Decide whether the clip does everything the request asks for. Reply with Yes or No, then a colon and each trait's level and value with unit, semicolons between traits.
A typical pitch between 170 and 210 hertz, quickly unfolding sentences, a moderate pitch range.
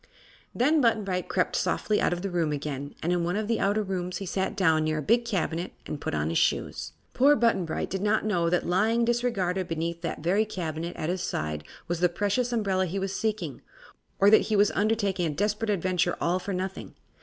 Yes: high, 190 Hz; fast, 220 wpm; average, 3.8 semitones